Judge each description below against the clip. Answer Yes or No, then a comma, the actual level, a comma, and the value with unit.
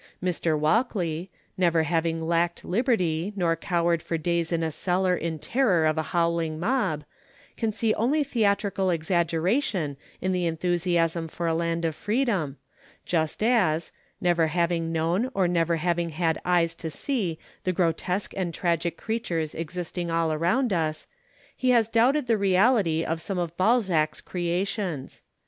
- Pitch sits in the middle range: Yes, medium, 175 Hz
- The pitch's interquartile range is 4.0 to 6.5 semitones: No, average, 3.0 semitones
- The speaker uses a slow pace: No, average, 150 wpm